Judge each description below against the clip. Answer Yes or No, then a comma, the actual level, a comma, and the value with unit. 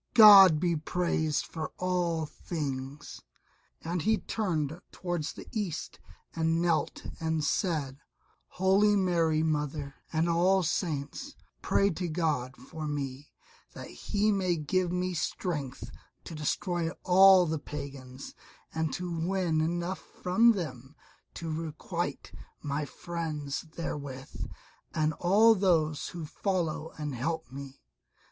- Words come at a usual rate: No, slow, 120 wpm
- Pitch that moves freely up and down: No, average, 3.3 semitones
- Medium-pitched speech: Yes, medium, 165 Hz